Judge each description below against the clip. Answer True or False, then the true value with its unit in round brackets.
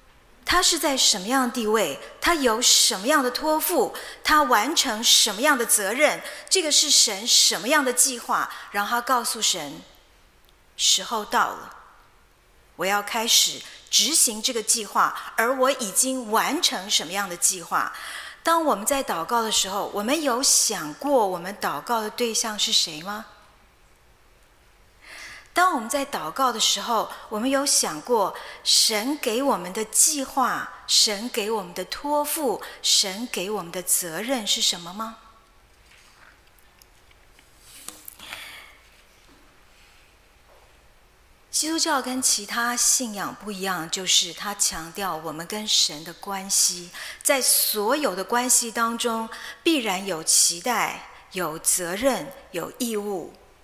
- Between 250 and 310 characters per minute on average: False (190 characters per minute)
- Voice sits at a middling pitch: False (230 Hz)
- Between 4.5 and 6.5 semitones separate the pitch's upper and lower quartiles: True (5.1 semitones)